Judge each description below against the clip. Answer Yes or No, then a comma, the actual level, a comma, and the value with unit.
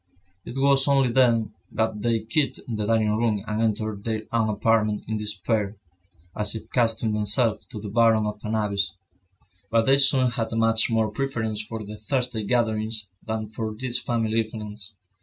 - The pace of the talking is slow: No, average, 170 wpm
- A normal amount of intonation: No, narrow, 1.6 semitones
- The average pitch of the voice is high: No, low, 110 Hz